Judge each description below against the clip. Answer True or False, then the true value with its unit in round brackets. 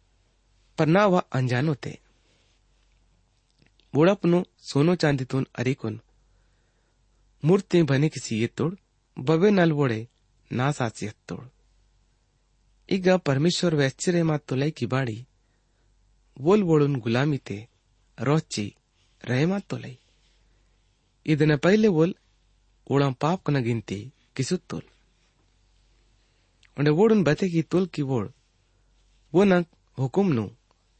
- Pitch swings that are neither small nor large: False (6.8 semitones)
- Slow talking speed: True (110 wpm)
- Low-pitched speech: True (125 Hz)